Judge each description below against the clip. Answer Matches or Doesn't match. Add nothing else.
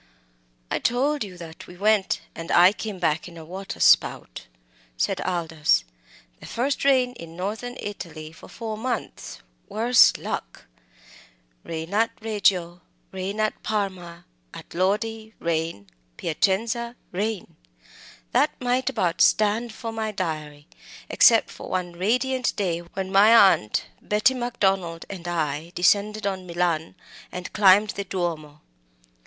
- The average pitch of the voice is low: Doesn't match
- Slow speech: Matches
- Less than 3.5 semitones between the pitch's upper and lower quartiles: Doesn't match